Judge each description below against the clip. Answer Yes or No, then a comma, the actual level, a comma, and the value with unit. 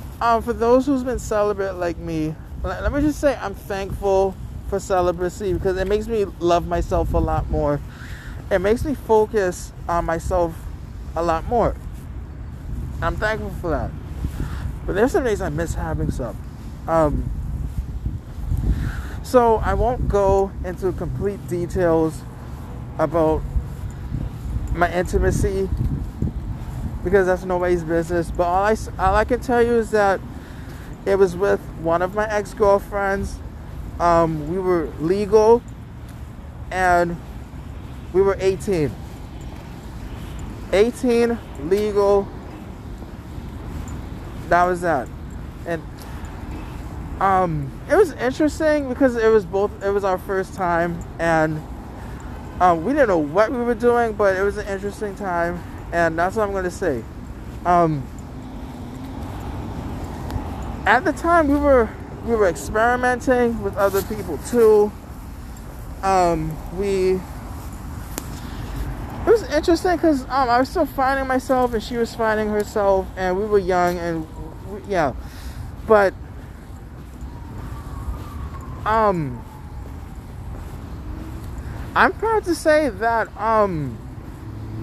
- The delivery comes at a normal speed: No, slow, 120 wpm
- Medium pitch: No, high, 195 Hz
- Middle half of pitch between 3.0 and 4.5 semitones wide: No, average, 5.0 semitones